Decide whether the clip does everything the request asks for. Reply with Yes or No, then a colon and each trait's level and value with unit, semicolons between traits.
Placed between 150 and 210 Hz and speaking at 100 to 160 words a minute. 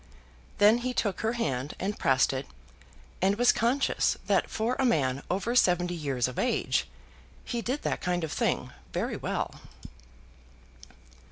Yes: high, 190 Hz; average, 150 wpm